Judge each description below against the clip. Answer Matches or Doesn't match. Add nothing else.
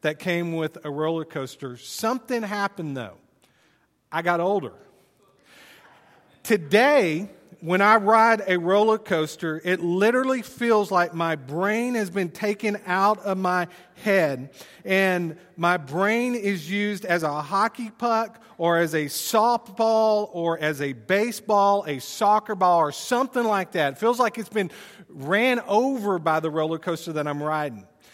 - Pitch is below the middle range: Doesn't match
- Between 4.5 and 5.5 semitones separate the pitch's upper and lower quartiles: Matches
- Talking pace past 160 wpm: Doesn't match